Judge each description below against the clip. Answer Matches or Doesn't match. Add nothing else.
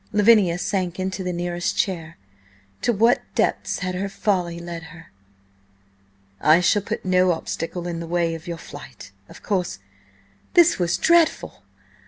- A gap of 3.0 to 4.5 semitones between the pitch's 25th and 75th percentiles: Doesn't match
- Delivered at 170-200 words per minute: Doesn't match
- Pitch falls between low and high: Matches